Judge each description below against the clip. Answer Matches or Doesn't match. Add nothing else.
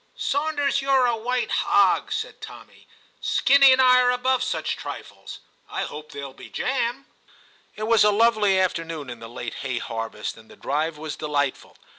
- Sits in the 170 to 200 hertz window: Doesn't match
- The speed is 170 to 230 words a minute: Matches